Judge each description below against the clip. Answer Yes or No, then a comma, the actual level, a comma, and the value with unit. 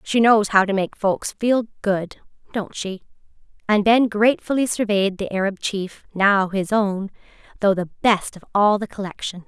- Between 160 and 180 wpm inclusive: Yes, average, 170 wpm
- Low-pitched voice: No, high, 205 Hz